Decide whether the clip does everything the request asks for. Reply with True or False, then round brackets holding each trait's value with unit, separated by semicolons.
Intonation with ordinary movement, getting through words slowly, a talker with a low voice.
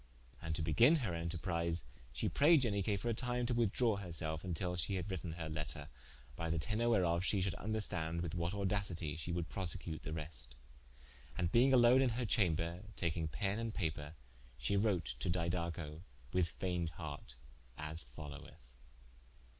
False (4.2 semitones; 170 wpm; 85 Hz)